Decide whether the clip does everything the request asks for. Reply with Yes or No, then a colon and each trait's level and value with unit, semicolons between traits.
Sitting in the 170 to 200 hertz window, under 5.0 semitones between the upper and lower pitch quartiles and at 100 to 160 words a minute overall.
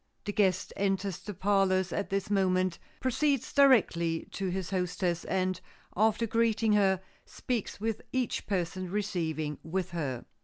Yes: high, 190 Hz; narrow, 2.6 semitones; average, 140 wpm